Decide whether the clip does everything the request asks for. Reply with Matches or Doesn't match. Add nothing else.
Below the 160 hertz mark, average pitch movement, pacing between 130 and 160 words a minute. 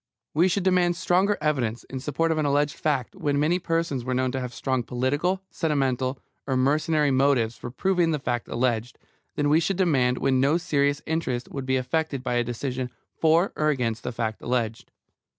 Doesn't match